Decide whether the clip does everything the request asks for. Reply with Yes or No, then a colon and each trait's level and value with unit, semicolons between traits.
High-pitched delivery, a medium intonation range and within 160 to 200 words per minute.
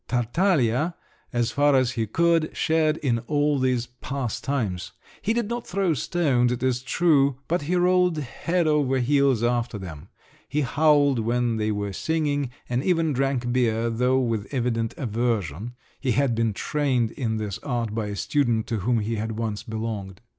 No: low, 125 Hz; average, 4.5 semitones; average, 170 wpm